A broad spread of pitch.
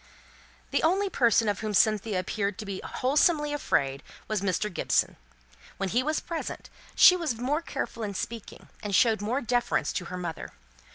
Yes: wide, 6.1 semitones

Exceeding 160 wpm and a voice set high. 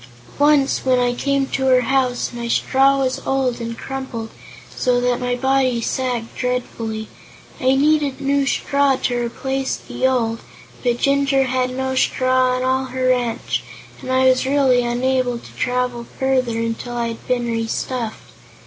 No: average, 155 wpm; very high, 255 Hz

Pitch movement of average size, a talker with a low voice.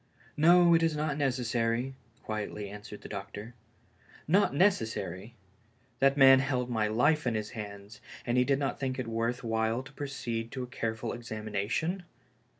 Yes: average, 3.9 semitones; low, 120 Hz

